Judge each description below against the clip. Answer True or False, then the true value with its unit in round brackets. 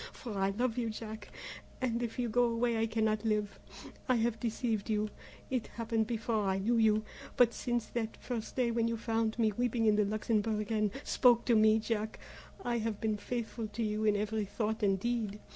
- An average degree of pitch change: False (1.7 semitones)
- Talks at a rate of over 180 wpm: True (200 wpm)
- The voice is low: False (220 Hz)